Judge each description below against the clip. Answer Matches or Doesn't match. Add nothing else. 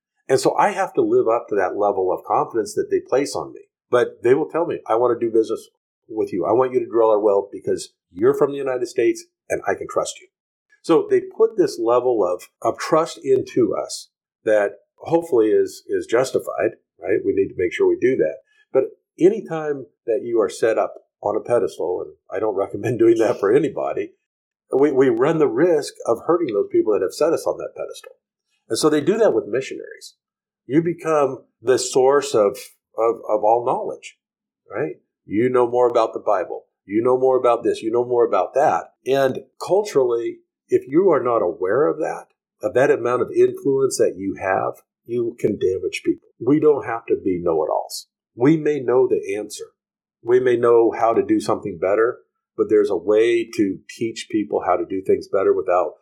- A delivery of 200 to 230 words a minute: Matches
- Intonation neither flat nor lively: Matches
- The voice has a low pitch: Doesn't match